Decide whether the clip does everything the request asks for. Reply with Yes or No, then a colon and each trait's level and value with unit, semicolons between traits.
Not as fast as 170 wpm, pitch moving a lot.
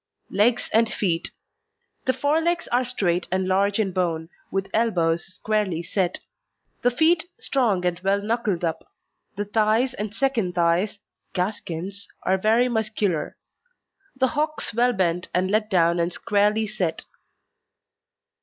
No: slow, 135 wpm; average, 4.3 semitones